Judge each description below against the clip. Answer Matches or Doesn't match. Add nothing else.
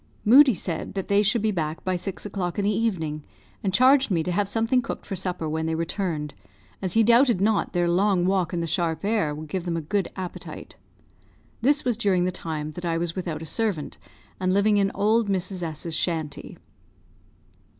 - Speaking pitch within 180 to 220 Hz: Matches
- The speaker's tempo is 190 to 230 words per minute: Matches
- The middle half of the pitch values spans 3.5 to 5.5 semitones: Matches